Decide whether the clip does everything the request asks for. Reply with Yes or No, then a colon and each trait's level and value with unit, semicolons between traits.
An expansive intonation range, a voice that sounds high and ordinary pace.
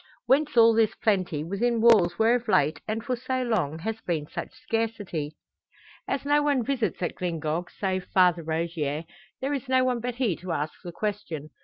Yes: wide, 6.5 semitones; high, 215 Hz; average, 185 wpm